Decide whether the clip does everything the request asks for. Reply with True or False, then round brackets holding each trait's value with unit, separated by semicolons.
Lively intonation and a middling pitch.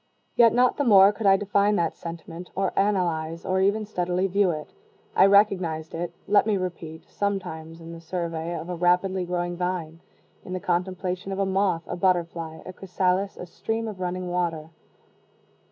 False (2.6 semitones; 180 Hz)